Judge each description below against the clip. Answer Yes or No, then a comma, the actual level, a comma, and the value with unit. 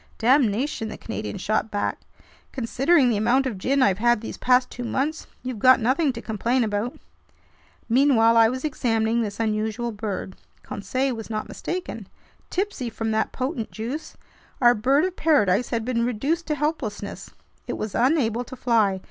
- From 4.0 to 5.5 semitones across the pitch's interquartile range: No, average, 3.4 semitones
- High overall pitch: Yes, high, 235 Hz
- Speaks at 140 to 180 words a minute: Yes, average, 165 wpm